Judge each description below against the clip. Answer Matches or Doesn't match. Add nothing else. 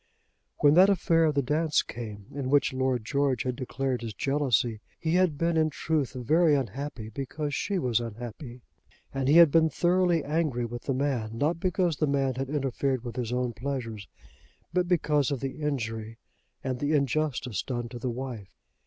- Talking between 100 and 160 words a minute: Doesn't match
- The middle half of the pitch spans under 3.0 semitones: Doesn't match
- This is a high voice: Doesn't match